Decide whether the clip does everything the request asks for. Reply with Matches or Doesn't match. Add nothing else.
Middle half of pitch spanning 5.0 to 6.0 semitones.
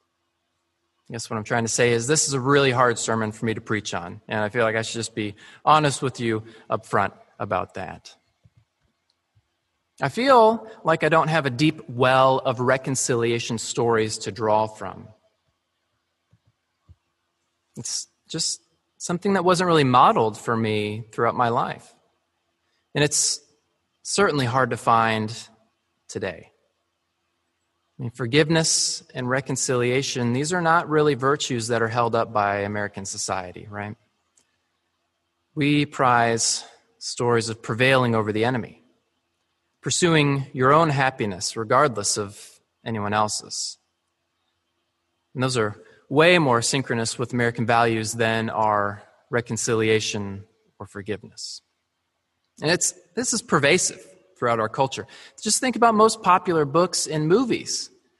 Matches